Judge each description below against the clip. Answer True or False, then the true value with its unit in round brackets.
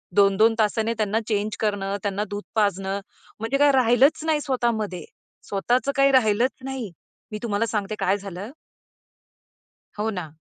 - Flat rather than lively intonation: False (3.3 semitones)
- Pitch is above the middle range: True (215 Hz)